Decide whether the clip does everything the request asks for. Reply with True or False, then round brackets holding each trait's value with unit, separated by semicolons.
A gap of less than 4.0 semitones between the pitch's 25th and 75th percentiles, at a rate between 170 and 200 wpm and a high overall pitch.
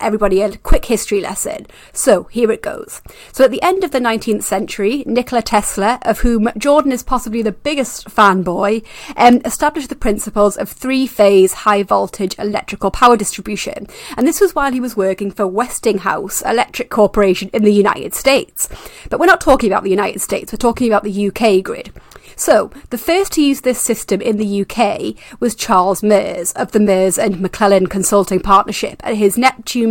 True (3.6 semitones; 180 wpm; 220 Hz)